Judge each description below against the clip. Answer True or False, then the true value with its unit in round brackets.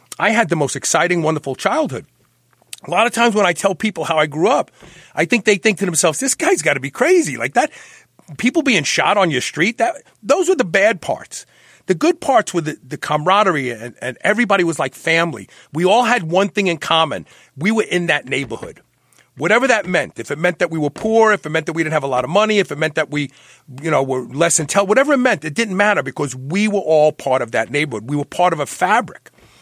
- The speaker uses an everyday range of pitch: False (5.9 semitones)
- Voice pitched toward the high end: False (175 Hz)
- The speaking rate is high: True (245 wpm)